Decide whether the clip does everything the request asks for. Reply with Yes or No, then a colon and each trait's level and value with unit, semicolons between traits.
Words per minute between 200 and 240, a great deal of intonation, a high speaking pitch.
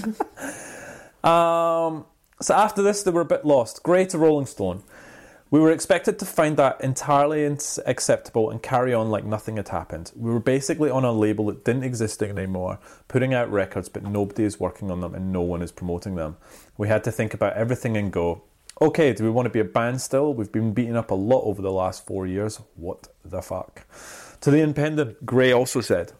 No: fast, 205 wpm; wide, 6.4 semitones; low, 115 Hz